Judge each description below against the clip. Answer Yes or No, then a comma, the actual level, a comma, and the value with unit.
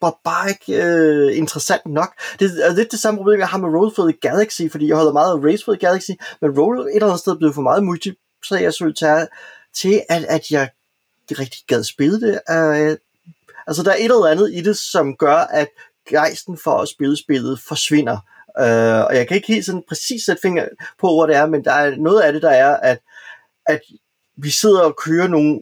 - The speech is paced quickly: Yes, fast, 230 wpm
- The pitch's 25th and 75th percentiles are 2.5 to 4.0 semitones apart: No, average, 4.7 semitones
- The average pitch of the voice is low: No, medium, 165 Hz